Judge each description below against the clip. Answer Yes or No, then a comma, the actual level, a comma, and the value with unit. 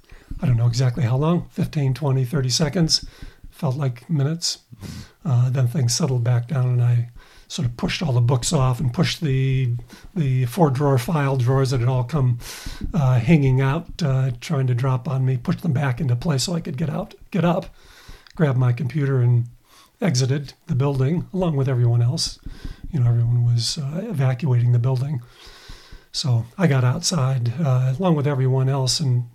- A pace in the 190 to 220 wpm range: No, average, 180 wpm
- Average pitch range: Yes, average, 3.7 semitones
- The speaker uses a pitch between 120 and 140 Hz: Yes, low, 135 Hz